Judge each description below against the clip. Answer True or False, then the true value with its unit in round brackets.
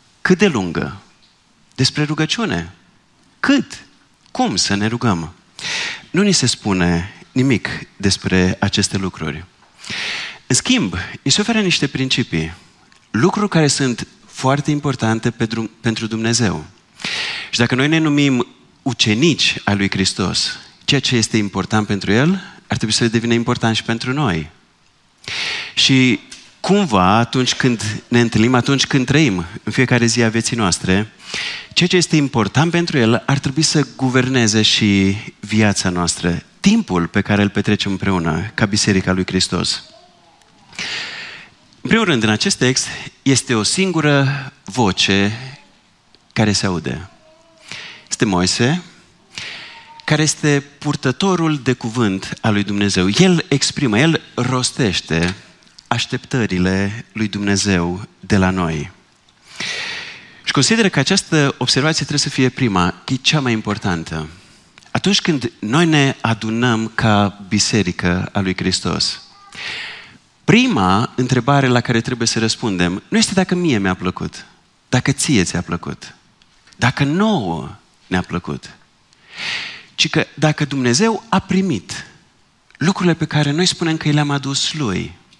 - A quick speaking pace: False (130 wpm)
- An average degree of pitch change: False (6.7 semitones)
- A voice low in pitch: True (120 Hz)